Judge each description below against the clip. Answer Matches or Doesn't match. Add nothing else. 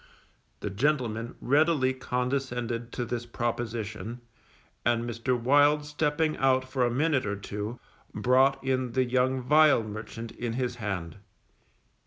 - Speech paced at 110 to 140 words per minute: Matches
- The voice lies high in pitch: Doesn't match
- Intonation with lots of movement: Doesn't match